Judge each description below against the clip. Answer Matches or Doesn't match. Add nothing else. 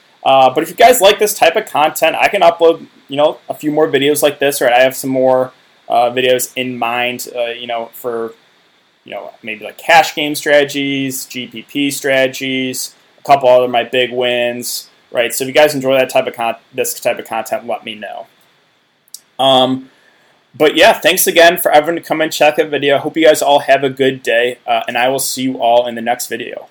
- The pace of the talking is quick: Matches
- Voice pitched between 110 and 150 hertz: Matches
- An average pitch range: Matches